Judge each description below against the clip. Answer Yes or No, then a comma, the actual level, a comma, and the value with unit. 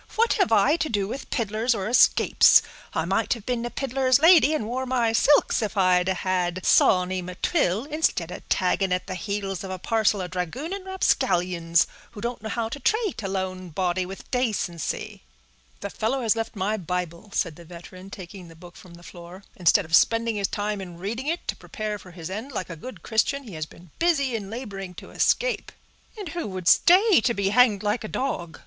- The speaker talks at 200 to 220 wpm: Yes, fast, 205 wpm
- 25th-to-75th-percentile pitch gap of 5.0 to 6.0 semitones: Yes, wide, 5.4 semitones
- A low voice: No, high, 205 Hz